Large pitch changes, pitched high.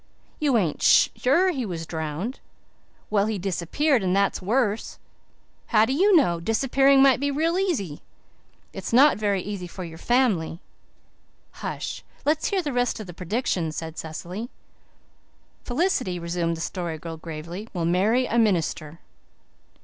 Yes: wide, 7.5 semitones; high, 205 Hz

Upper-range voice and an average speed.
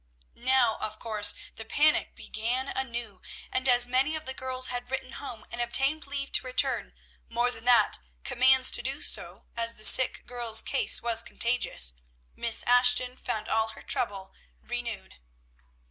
Yes: high, 245 Hz; average, 160 wpm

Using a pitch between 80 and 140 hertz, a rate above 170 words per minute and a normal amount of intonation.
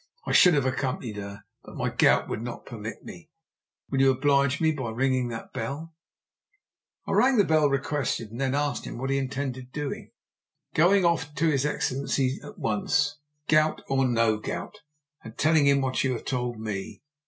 Yes: low, 135 Hz; average, 180 wpm; average, 3.3 semitones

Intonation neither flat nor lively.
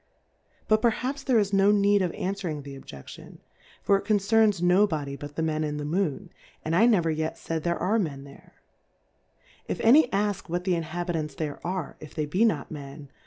Yes: average, 5.0 semitones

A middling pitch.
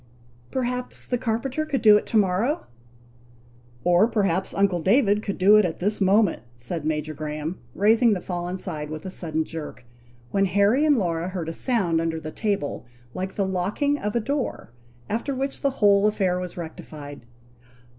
No: high, 195 Hz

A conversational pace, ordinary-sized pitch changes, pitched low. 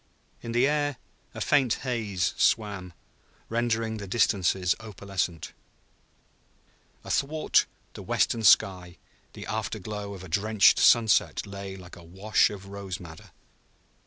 No: slow, 125 wpm; average, 3.5 semitones; low, 100 Hz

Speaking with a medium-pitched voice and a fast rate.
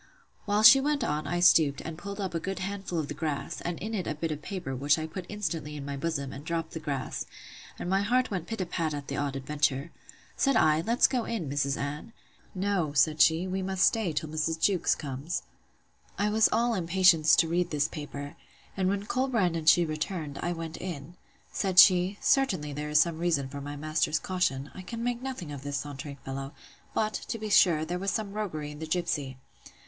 Yes: medium, 165 Hz; fast, 215 wpm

